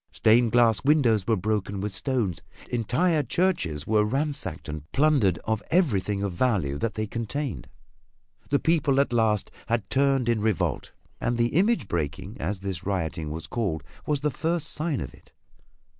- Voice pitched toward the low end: Yes, low, 115 Hz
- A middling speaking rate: Yes, average, 160 wpm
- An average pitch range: No, wide, 6.2 semitones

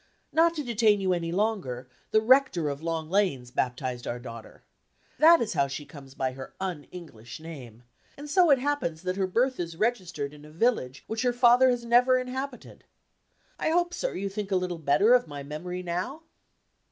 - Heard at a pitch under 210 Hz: Yes, medium, 185 Hz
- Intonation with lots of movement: Yes, wide, 8.9 semitones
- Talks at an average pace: Yes, average, 190 wpm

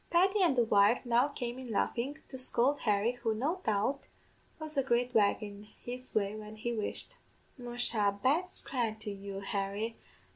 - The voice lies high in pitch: Yes, high, 235 Hz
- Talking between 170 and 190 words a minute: Yes, average, 175 wpm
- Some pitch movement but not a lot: Yes, average, 3.8 semitones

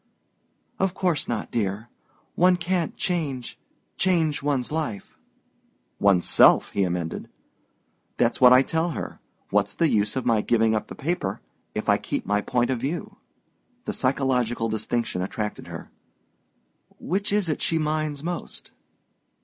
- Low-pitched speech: Yes, low, 130 Hz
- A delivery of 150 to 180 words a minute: No, average, 140 wpm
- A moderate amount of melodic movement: No, wide, 6.8 semitones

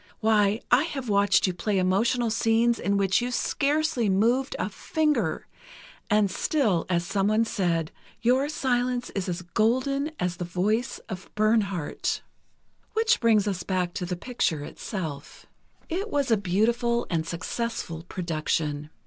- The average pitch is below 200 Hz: No, high, 210 Hz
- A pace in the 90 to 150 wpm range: Yes, average, 140 wpm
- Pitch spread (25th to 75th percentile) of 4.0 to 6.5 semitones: Yes, average, 5.1 semitones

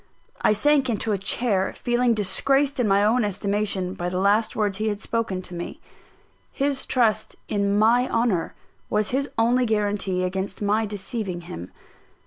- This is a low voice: No, high, 210 Hz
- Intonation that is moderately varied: Yes, average, 3.4 semitones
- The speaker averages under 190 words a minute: Yes, average, 160 wpm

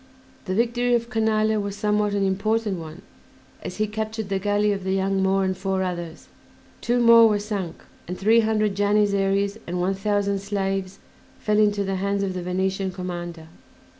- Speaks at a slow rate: No, average, 175 wpm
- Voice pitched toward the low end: No, high, 200 Hz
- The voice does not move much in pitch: Yes, narrow, 1.9 semitones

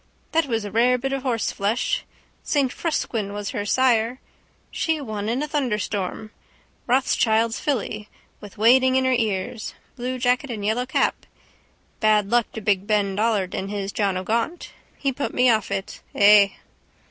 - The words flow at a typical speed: Yes, average, 160 wpm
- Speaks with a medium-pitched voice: No, high, 225 Hz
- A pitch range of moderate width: Yes, average, 3.7 semitones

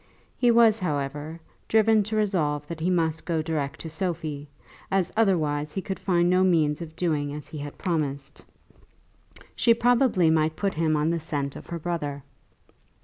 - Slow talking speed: No, average, 170 wpm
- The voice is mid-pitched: Yes, medium, 165 Hz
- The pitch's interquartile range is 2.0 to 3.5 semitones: No, average, 4.0 semitones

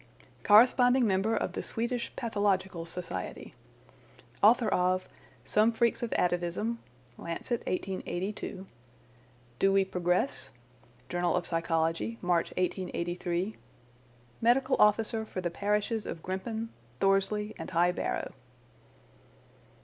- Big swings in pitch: No, average, 4.0 semitones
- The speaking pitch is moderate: No, high, 195 Hz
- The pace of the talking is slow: Yes, slow, 105 wpm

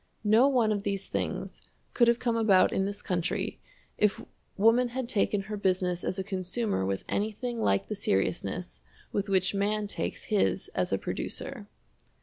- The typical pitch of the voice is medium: No, high, 205 Hz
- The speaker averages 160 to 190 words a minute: Yes, average, 165 wpm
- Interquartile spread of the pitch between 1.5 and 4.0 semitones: Yes, average, 3.2 semitones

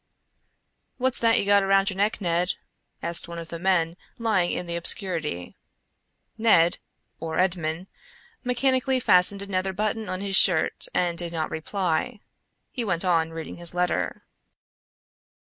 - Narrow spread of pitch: No, average, 3.2 semitones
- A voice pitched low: No, medium, 185 Hz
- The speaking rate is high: No, slow, 135 wpm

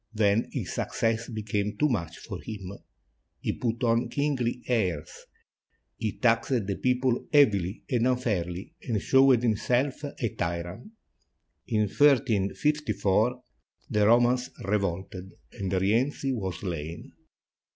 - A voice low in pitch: Yes, low, 110 Hz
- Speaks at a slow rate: Yes, slow, 120 wpm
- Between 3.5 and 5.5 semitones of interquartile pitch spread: Yes, average, 4.4 semitones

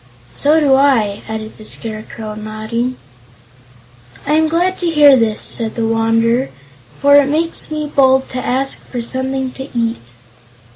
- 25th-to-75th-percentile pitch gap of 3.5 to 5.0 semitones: Yes, average, 4.1 semitones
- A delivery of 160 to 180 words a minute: No, average, 150 wpm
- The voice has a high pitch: Yes, very high, 255 Hz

